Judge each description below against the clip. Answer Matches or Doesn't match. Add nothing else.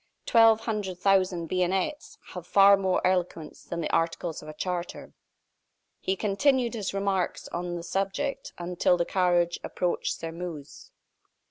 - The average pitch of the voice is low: Doesn't match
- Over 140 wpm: Doesn't match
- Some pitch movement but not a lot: Doesn't match